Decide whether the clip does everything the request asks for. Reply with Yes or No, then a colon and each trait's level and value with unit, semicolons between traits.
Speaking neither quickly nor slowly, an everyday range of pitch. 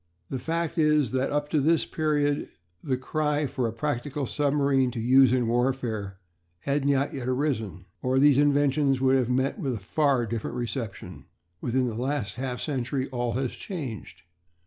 Yes: average, 170 wpm; average, 3.0 semitones